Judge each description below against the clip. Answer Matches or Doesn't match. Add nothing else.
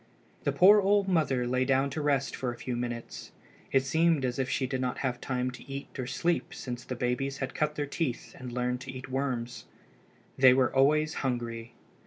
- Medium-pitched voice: Doesn't match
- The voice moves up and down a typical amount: Doesn't match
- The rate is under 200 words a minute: Doesn't match